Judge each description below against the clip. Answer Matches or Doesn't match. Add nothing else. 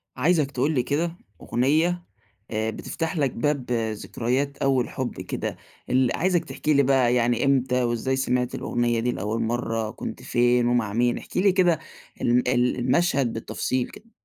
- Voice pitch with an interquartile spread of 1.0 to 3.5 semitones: Matches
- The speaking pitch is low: Matches